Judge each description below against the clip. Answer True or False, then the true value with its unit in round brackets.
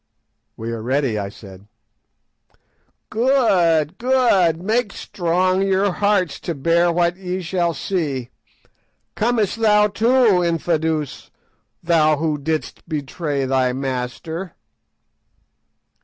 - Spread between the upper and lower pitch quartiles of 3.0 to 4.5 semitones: False (5.0 semitones)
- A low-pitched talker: False (170 Hz)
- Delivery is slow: True (105 wpm)